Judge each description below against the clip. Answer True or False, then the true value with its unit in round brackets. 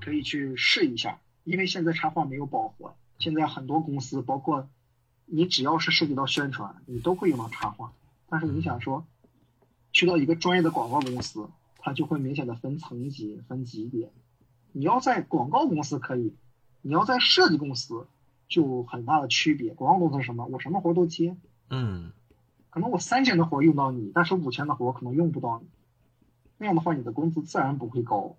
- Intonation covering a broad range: False (4.6 semitones)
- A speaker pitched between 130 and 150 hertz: True (140 Hz)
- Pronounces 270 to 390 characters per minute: True (295 characters per minute)